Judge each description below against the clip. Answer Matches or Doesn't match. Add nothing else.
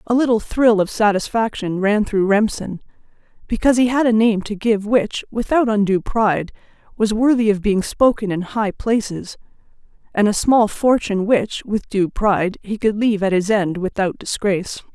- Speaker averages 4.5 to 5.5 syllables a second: Matches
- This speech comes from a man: Doesn't match